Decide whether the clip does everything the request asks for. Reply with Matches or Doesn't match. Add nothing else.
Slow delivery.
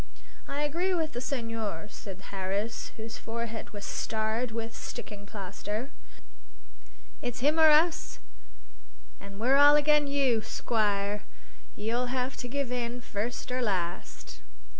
Matches